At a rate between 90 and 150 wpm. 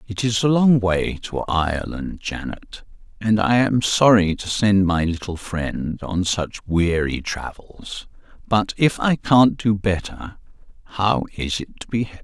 No: average, 160 wpm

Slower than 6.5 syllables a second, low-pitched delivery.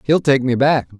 Yes: 4.9 syllables/s; low, 130 Hz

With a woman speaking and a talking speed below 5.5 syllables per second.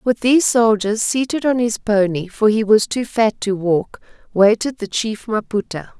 Yes: female; 4.5 syllables/s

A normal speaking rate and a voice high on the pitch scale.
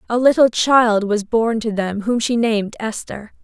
Yes: average, 190 wpm; high, 225 Hz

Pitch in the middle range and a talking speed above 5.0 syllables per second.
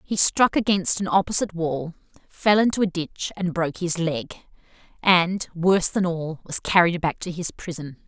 No: medium, 175 Hz; 4.7 syllables/s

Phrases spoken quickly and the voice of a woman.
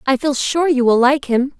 Yes: fast, 265 wpm; female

